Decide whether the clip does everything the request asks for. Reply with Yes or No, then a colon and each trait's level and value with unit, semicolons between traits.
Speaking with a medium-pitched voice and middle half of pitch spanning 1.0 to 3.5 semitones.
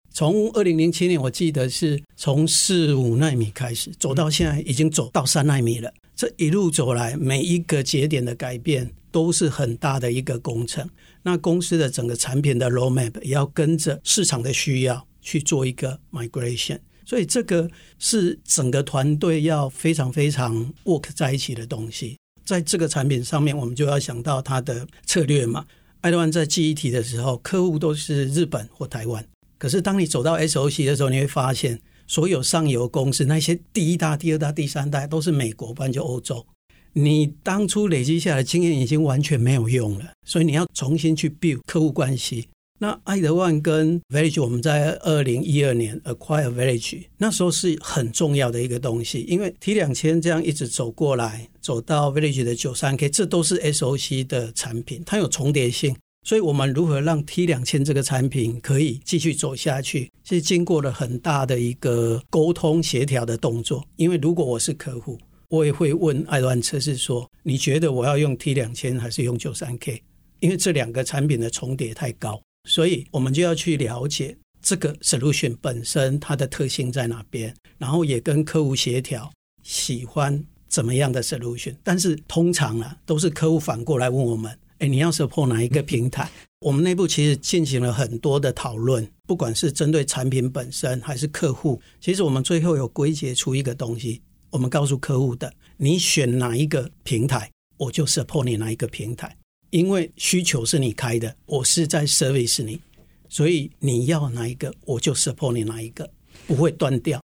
No: medium, 145 Hz; average, 4.2 semitones